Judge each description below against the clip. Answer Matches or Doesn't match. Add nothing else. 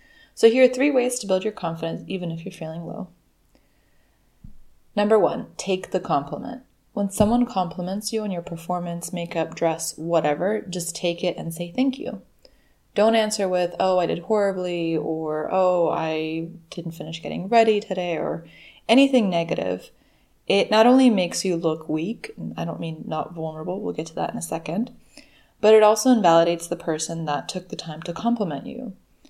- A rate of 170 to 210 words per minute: Matches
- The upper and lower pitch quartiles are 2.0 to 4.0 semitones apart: Doesn't match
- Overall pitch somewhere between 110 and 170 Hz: Doesn't match